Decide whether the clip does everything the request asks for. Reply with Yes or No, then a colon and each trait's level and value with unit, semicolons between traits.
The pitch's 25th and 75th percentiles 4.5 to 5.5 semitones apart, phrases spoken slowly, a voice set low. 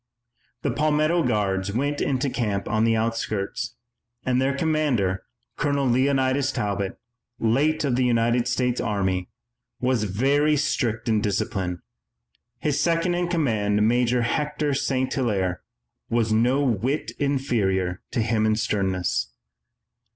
Yes: average, 5.0 semitones; slow, 125 wpm; low, 120 Hz